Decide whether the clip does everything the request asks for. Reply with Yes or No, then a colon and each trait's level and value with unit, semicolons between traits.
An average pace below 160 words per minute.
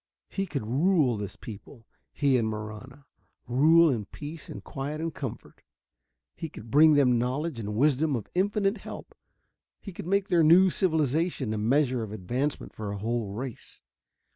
No: average, 165 wpm